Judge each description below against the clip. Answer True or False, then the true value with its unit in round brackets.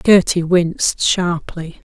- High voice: False (175 Hz)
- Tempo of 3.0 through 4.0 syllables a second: True (3.5 syllables/s)